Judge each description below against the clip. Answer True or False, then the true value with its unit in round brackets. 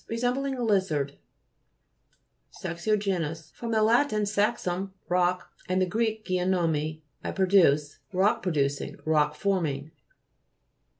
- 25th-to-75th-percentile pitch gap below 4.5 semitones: False (4.8 semitones)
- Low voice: False (185 Hz)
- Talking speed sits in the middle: False (95 wpm)